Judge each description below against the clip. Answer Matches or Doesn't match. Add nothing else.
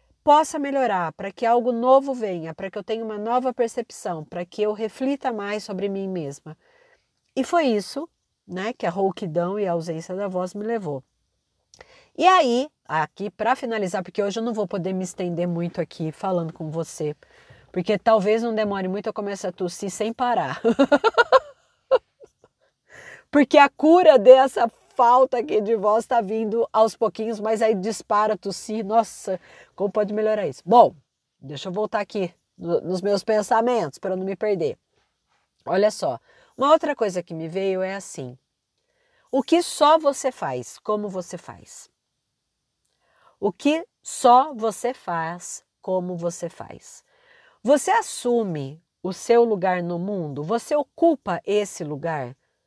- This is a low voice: Doesn't match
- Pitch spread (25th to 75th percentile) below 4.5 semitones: Doesn't match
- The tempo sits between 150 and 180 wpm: Matches